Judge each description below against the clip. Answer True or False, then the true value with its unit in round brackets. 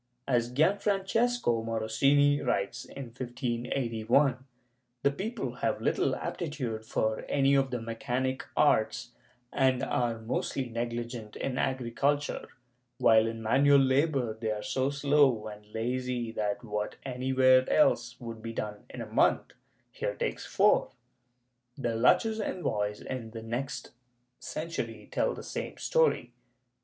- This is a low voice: True (125 Hz)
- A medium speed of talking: False (125 wpm)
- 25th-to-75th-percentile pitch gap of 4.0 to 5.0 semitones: False (3.5 semitones)